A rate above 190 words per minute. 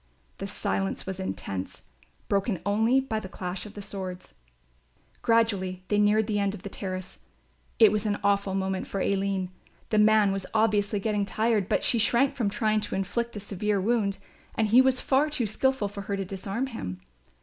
No: average, 185 wpm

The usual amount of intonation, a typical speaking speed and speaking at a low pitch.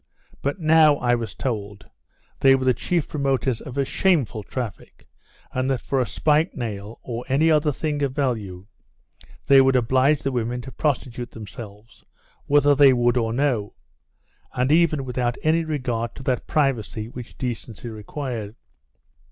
Yes: average, 3.6 semitones; average, 155 wpm; low, 130 Hz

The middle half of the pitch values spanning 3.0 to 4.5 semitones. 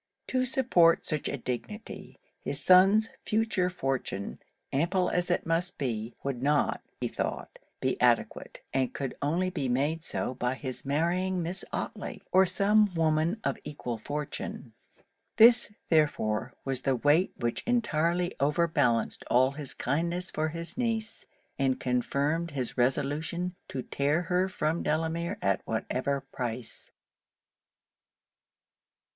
No: average, 5.1 semitones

